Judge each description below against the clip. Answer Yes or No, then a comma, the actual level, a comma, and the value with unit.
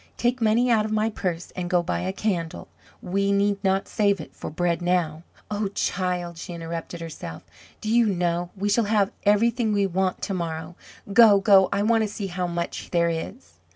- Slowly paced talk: No, average, 195 wpm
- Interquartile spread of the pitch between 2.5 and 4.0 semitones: Yes, average, 3.3 semitones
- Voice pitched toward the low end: No, high, 190 Hz